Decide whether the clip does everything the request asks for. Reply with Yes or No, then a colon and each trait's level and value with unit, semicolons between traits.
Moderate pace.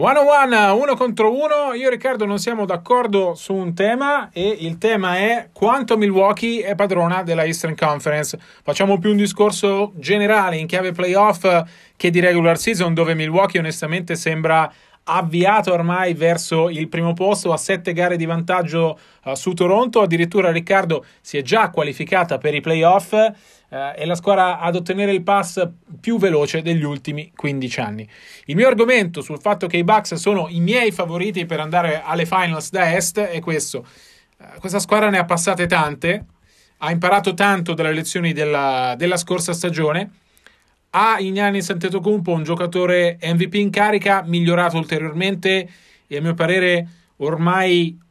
Yes: average, 160 wpm